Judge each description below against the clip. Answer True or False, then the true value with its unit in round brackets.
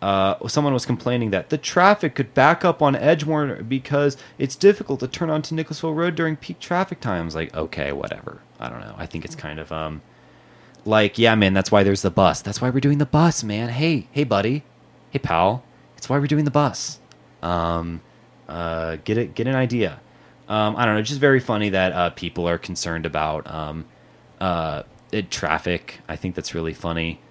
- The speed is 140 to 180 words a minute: False (200 wpm)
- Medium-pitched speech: False (110 Hz)